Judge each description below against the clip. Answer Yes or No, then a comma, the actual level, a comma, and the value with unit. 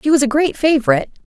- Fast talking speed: Yes, fast, 235 wpm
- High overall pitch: Yes, very high, 270 Hz